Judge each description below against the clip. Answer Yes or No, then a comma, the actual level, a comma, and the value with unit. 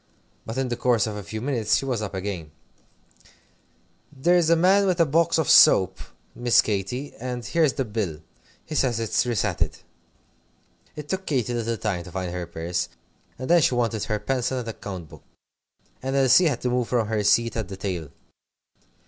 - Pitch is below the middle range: Yes, low, 120 Hz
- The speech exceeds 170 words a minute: Yes, average, 190 wpm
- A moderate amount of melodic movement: Yes, average, 4.7 semitones